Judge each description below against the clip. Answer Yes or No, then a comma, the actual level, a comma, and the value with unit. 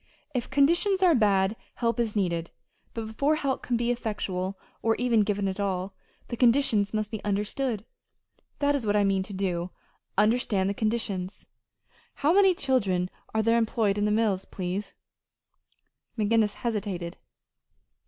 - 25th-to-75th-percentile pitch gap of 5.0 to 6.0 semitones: No, average, 3.4 semitones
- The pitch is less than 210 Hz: No, high, 215 Hz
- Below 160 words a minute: Yes, average, 150 wpm